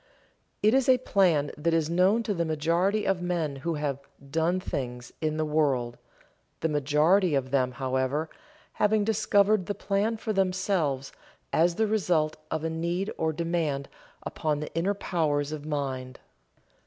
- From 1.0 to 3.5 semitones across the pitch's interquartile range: No, average, 4.7 semitones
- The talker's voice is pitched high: No, medium, 165 Hz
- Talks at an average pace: Yes, average, 155 wpm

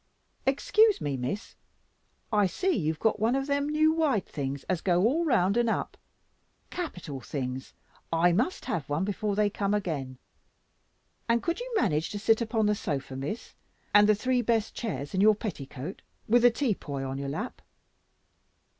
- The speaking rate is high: No, average, 175 wpm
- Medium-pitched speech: No, high, 205 Hz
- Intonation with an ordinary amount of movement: No, wide, 8.1 semitones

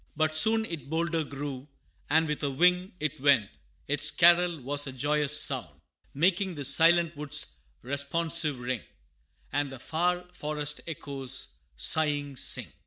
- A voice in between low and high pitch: Yes, medium, 150 Hz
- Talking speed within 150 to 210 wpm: No, average, 140 wpm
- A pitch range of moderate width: Yes, average, 3.0 semitones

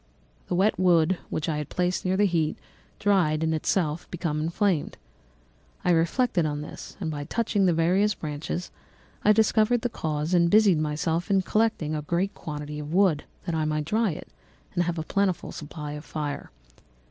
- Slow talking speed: No, average, 180 wpm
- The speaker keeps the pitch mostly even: No, average, 4.0 semitones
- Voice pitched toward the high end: No, medium, 170 Hz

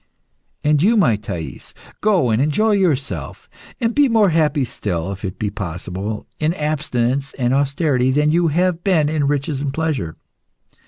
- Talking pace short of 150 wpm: No, average, 160 wpm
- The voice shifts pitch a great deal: Yes, wide, 5.7 semitones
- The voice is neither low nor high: Yes, medium, 145 Hz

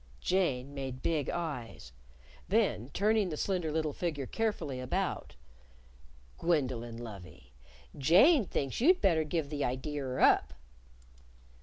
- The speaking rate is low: Yes, slow, 120 wpm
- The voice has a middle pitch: Yes, medium, 150 Hz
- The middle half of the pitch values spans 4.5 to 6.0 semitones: Yes, wide, 5.6 semitones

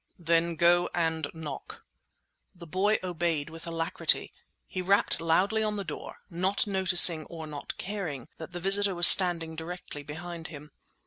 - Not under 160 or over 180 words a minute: No, average, 150 wpm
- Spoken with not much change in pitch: Yes, narrow, 2.3 semitones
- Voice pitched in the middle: Yes, medium, 170 Hz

